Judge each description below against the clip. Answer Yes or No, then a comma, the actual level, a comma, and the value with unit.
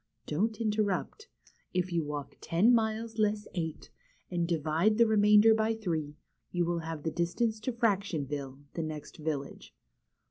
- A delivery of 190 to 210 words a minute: No, average, 145 wpm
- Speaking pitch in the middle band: Yes, medium, 180 Hz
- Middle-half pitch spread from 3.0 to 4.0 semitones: No, wide, 5.4 semitones